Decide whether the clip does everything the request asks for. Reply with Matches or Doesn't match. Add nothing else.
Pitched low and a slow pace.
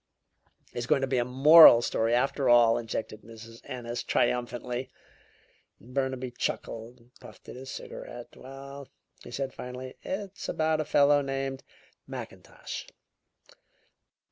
Matches